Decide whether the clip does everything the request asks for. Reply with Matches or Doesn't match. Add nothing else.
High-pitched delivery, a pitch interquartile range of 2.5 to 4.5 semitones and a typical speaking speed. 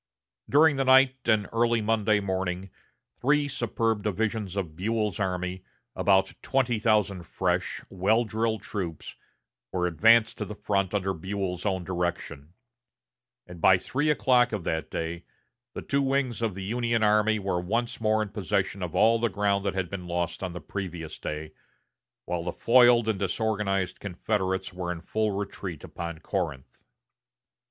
Doesn't match